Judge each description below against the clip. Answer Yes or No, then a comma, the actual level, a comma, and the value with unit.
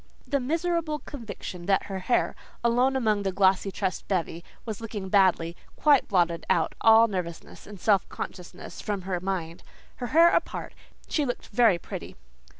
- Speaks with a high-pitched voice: Yes, high, 200 Hz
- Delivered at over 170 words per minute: No, average, 155 wpm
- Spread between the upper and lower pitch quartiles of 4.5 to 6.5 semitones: Yes, average, 4.9 semitones